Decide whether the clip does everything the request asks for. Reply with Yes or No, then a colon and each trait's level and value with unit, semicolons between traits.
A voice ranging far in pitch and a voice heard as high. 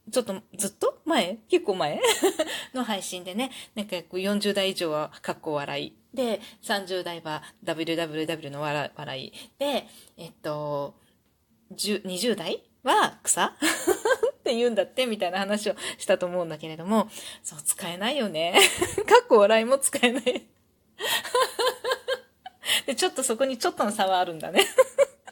Yes: wide, 9.0 semitones; high, 215 Hz